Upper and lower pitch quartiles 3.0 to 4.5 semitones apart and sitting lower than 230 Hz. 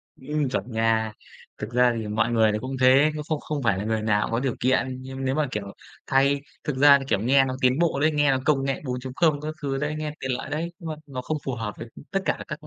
Yes: average, 3.9 semitones; low, 135 Hz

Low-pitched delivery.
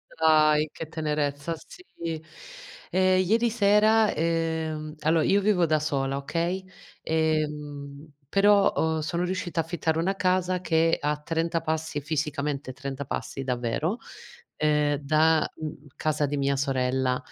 No: medium, 155 Hz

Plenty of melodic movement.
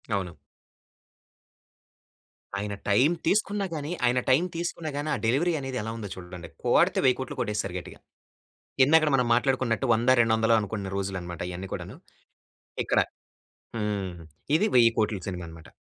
Yes: wide, 6.0 semitones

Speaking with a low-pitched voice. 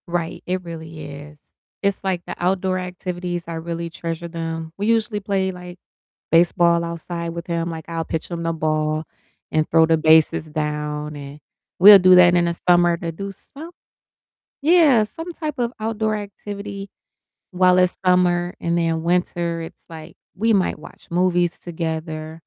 No: medium, 175 Hz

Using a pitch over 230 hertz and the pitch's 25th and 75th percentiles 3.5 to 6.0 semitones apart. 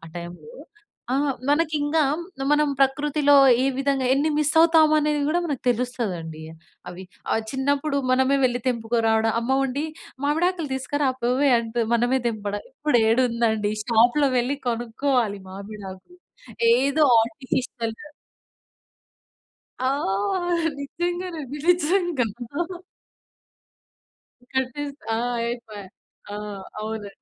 Yes: very high, 260 Hz; average, 4.5 semitones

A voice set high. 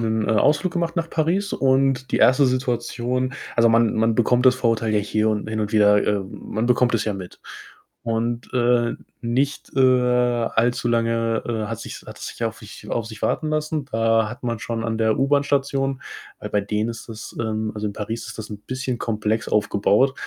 No: low, 115 Hz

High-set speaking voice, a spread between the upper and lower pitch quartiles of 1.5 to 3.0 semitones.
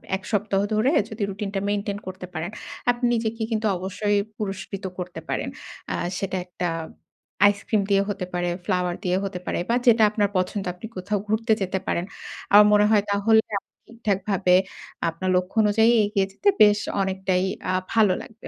Yes: high, 200 Hz; narrow, 2.4 semitones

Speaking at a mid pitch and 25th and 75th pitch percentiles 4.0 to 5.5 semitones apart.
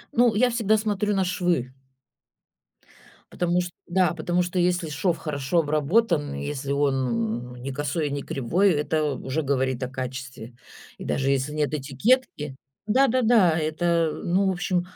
Yes: medium, 155 Hz; average, 5.0 semitones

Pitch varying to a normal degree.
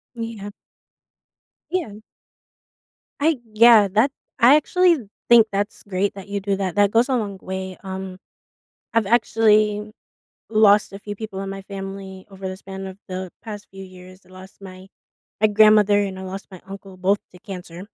No: narrow, 2.2 semitones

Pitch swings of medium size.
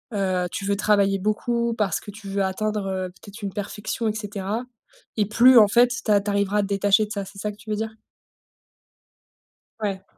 No: narrow, 1.5 semitones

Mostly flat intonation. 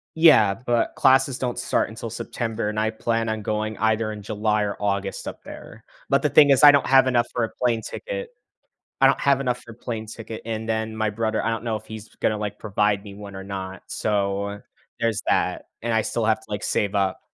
Yes: narrow, 2.2 semitones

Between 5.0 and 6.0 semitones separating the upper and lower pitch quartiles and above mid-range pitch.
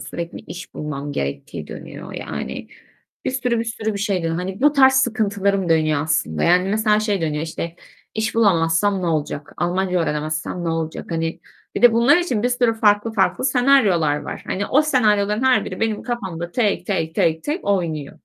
Yes: wide, 5.6 semitones; high, 195 Hz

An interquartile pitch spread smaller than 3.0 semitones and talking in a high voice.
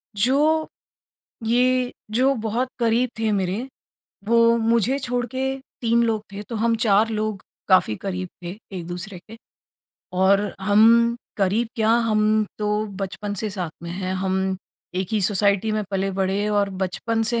No: average, 3.3 semitones; high, 215 Hz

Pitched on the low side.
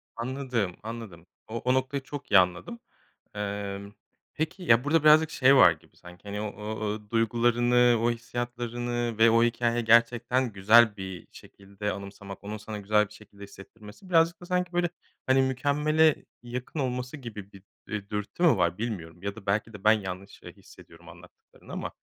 Yes: low, 115 Hz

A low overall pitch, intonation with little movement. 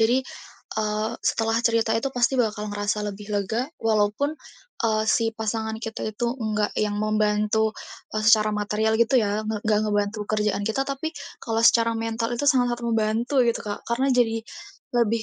No: high, 220 Hz; narrow, 1.5 semitones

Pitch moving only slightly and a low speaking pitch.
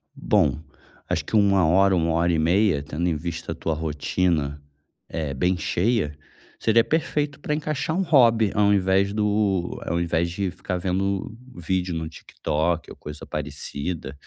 No: average, 4.2 semitones; very low, 90 Hz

